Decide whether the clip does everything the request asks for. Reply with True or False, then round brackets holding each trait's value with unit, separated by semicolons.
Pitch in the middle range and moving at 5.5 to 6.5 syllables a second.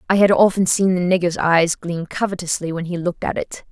True (175 Hz; 5.8 syllables/s)